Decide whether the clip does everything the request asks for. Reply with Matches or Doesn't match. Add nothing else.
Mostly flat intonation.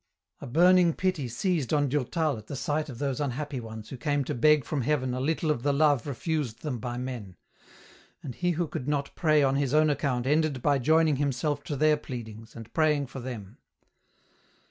Doesn't match